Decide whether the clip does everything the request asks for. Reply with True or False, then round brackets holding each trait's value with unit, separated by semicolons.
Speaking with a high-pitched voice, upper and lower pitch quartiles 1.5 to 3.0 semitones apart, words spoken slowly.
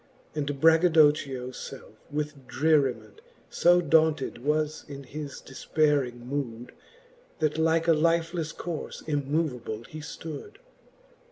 False (150 Hz; 2.7 semitones; 105 wpm)